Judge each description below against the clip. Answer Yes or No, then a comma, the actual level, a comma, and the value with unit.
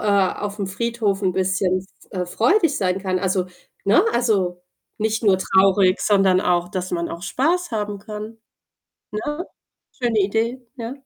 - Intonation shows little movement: No, average, 3.3 semitones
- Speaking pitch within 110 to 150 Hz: No, high, 200 Hz